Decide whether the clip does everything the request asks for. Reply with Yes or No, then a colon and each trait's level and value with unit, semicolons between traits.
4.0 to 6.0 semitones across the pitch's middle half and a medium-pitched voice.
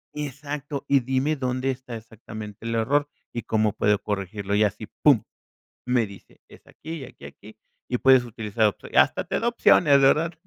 No: average, 4.6 semitones; low, 125 Hz